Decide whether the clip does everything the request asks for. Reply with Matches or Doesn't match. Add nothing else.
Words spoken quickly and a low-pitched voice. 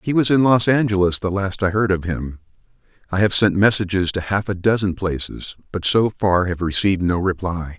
Matches